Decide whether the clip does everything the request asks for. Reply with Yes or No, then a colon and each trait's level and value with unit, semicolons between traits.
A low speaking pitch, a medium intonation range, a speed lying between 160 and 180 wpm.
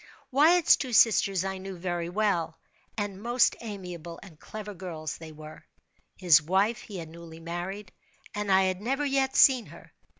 No: high, 190 Hz; average, 4.2 semitones; average, 165 wpm